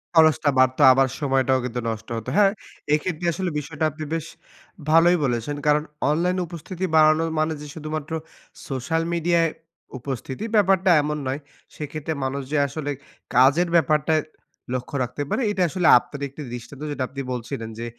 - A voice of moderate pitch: Yes, medium, 150 Hz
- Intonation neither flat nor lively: Yes, average, 3.6 semitones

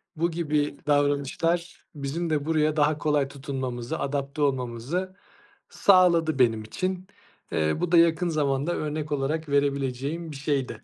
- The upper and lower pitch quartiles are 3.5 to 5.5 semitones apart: No, average, 3.1 semitones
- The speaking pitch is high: No, medium, 145 Hz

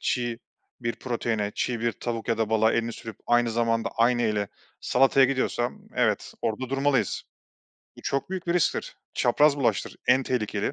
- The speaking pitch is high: No, low, 120 Hz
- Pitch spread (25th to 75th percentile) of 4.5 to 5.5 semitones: No, narrow, 2.5 semitones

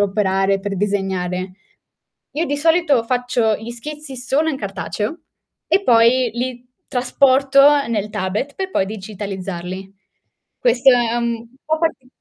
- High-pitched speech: Yes, high, 235 Hz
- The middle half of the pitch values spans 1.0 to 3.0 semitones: No, wide, 5.6 semitones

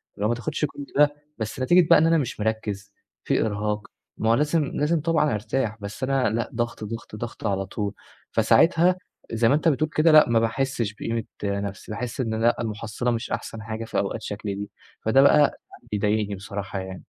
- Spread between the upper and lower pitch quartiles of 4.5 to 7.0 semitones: Yes, average, 4.8 semitones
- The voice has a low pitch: Yes, low, 115 Hz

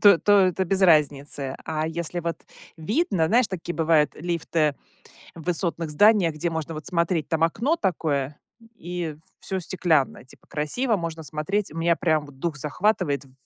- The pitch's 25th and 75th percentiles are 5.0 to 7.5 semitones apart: No, average, 3.2 semitones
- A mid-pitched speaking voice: Yes, medium, 165 Hz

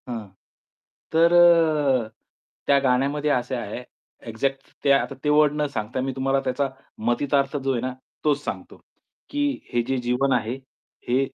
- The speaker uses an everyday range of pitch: No, narrow, 2.3 semitones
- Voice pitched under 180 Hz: Yes, low, 135 Hz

